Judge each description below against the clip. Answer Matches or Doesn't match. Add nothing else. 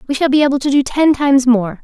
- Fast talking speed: Matches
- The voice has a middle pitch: Doesn't match